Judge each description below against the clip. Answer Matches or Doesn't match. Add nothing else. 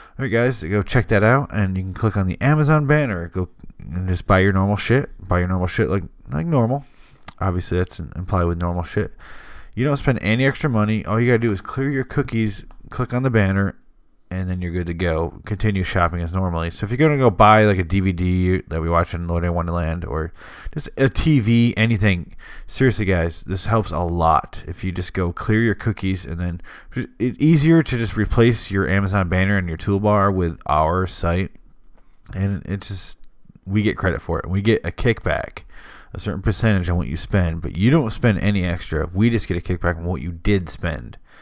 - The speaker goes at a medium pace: Doesn't match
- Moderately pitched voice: Doesn't match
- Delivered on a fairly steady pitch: Doesn't match